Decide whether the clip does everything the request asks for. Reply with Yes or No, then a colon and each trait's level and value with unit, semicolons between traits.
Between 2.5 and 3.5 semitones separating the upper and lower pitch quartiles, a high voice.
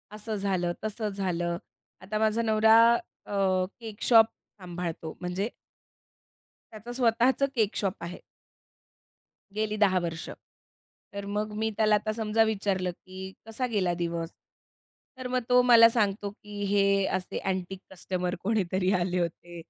Yes: average, 3.1 semitones; high, 200 Hz